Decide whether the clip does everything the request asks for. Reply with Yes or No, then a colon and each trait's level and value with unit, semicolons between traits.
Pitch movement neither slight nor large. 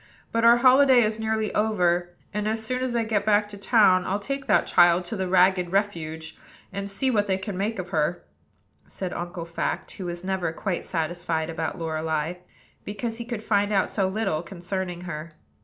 Yes: average, 3.9 semitones